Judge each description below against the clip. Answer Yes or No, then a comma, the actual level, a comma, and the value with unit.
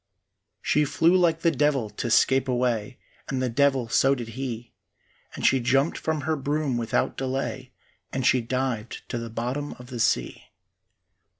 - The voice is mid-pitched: No, low, 130 Hz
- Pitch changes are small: No, average, 3.0 semitones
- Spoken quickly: No, average, 165 wpm